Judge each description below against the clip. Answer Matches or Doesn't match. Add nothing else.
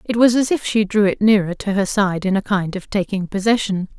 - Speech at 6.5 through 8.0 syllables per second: Doesn't match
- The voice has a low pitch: Doesn't match